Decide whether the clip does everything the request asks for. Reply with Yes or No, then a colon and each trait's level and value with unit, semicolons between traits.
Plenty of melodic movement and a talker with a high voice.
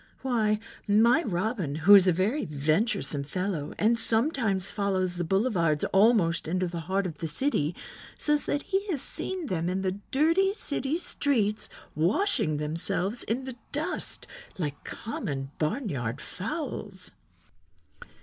Yes: wide, 7.1 semitones; high, 200 Hz